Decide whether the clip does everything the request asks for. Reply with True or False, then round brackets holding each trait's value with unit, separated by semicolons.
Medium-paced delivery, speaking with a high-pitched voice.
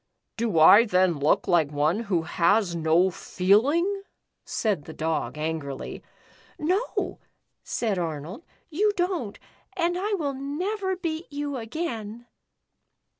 False (130 wpm; 220 Hz)